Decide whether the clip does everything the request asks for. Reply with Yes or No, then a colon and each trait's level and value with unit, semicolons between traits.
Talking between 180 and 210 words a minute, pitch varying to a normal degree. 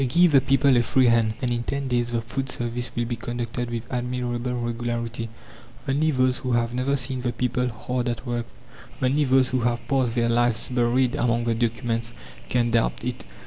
No: average, 195 wpm; narrow, 1.5 semitones